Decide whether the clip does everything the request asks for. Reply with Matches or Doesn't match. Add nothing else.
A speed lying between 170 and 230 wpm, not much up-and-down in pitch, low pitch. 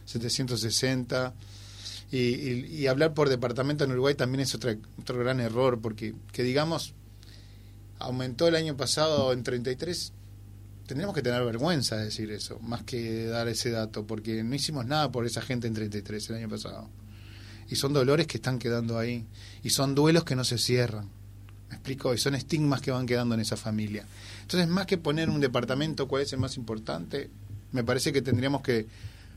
Doesn't match